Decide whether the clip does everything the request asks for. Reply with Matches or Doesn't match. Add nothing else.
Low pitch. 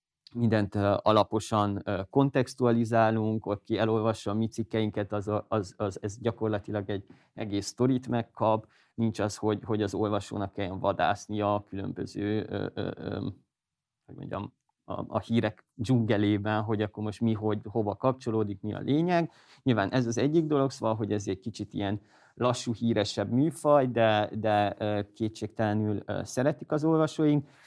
Matches